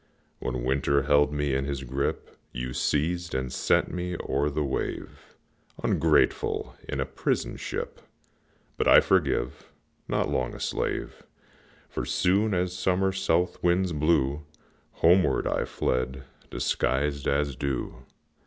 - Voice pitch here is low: Yes, very low, 70 Hz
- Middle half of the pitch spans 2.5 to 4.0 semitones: No, average, 4.8 semitones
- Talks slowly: Yes, slow, 130 wpm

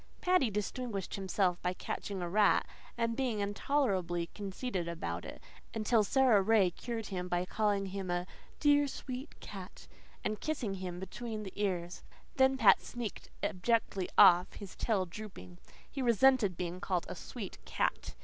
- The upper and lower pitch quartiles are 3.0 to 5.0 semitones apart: Yes, average, 4.4 semitones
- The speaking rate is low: No, average, 150 wpm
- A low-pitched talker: No, high, 200 Hz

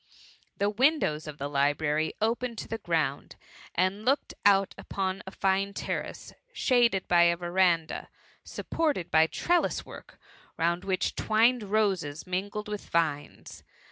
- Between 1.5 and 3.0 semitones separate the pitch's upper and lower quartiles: No, average, 4.7 semitones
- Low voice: No, high, 190 Hz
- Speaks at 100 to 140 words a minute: Yes, slow, 135 wpm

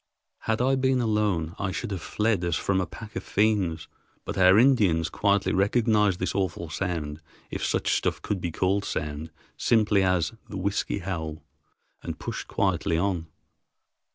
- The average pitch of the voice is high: No, very low, 95 Hz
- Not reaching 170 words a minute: Yes, average, 160 wpm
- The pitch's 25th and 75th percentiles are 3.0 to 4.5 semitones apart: Yes, average, 3.8 semitones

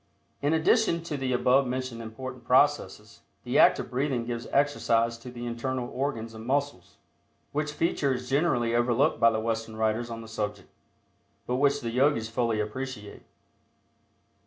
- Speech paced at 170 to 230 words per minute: No, average, 160 wpm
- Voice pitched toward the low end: Yes, low, 125 Hz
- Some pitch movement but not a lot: Yes, average, 3.3 semitones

